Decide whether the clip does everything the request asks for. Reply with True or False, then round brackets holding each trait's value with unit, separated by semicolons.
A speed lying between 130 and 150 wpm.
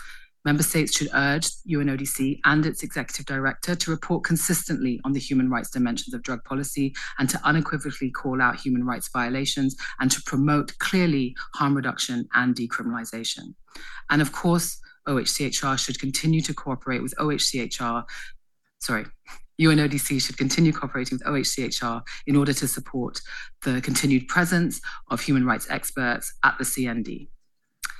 True (145 wpm)